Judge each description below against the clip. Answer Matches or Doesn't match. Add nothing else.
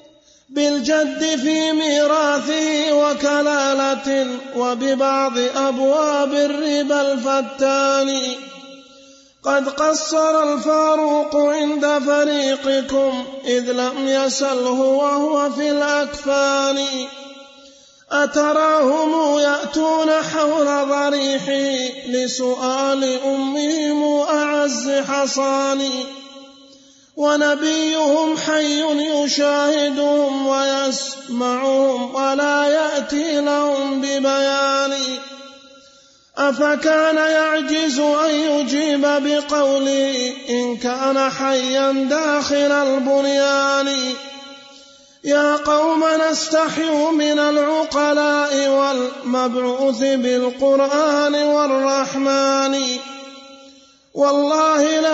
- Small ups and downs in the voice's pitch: Matches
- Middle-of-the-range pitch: Doesn't match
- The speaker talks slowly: Matches